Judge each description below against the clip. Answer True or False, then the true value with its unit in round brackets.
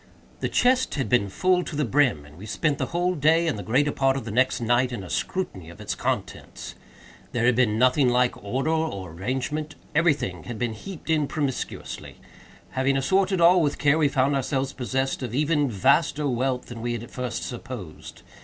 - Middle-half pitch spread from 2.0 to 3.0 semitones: False (4.3 semitones)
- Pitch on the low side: True (130 Hz)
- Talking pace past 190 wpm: True (200 wpm)